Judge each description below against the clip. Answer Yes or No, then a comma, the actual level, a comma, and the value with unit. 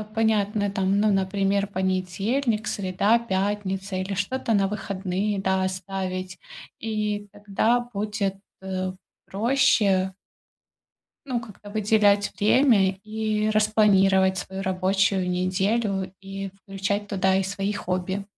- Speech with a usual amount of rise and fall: No, narrow, 1.9 semitones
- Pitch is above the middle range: Yes, high, 200 Hz